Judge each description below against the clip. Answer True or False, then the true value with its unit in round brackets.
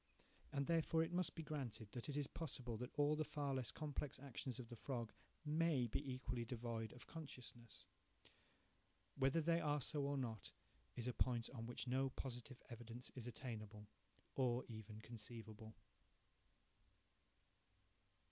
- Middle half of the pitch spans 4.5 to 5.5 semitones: False (3.7 semitones)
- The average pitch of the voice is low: True (125 Hz)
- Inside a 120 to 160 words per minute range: True (145 wpm)